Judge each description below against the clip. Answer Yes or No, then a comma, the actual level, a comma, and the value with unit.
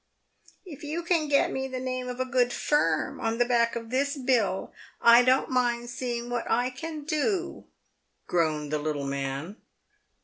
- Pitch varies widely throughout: No, average, 3.0 semitones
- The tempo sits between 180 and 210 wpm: No, average, 170 wpm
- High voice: Yes, high, 245 Hz